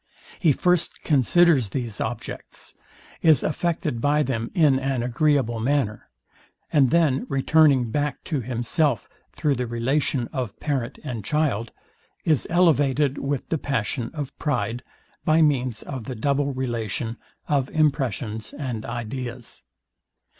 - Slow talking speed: Yes, slow, 125 wpm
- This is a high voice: No, low, 135 Hz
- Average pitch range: Yes, average, 3.8 semitones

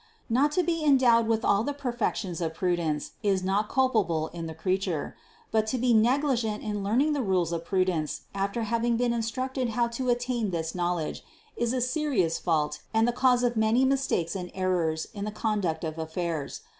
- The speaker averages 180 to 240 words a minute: Yes, average, 190 wpm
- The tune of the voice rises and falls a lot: Yes, wide, 5.8 semitones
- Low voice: No, high, 215 Hz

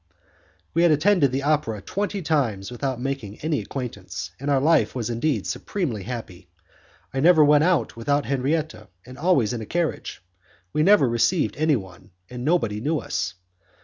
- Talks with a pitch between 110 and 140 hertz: Yes, low, 135 Hz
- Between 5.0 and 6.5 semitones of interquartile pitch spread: Yes, average, 5.3 semitones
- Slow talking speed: No, average, 160 wpm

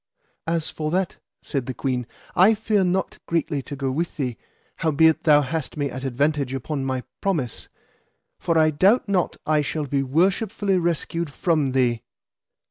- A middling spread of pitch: Yes, average, 4.3 semitones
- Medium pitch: Yes, medium, 155 Hz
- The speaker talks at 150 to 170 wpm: Yes, average, 160 wpm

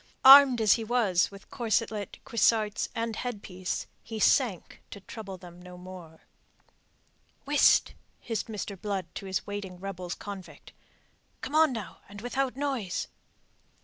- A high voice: Yes, high, 205 Hz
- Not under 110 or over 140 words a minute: Yes, slow, 135 wpm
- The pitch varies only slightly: No, average, 4.1 semitones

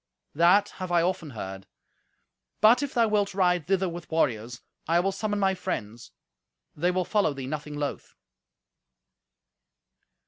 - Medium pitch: Yes, medium, 175 Hz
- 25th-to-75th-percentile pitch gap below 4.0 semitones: No, average, 4.9 semitones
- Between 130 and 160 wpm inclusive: Yes, average, 140 wpm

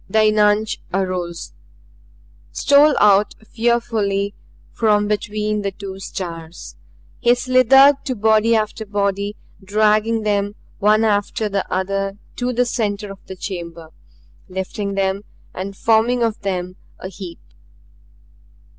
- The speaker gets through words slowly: Yes, slow, 120 wpm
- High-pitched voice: Yes, high, 205 Hz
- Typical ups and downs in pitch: No, narrow, 2.3 semitones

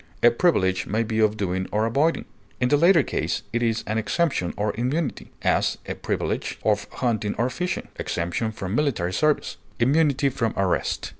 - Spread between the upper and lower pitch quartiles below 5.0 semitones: No, average, 5.3 semitones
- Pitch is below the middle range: Yes, low, 115 Hz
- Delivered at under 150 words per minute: No, average, 170 wpm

